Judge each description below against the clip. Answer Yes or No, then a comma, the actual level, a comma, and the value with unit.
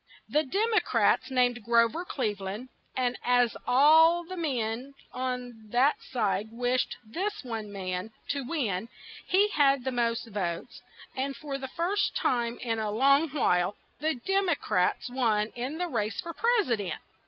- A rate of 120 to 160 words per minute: No, average, 170 wpm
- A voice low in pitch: No, very high, 250 Hz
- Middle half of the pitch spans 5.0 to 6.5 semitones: Yes, average, 5.3 semitones